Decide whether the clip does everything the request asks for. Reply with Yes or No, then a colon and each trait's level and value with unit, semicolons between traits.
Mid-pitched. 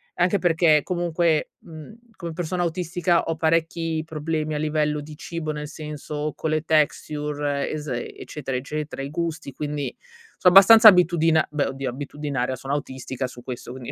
Yes: medium, 155 Hz